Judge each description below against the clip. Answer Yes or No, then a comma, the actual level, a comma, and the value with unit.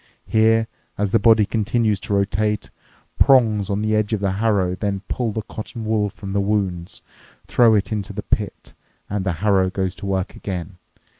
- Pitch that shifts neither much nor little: No, narrow, 2.0 semitones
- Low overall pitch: Yes, low, 105 Hz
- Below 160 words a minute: No, average, 180 wpm